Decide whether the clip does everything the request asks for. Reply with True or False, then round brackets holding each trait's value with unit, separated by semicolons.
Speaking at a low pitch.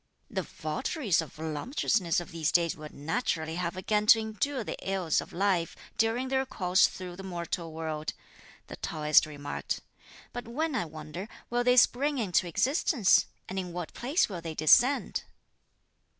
False (185 Hz)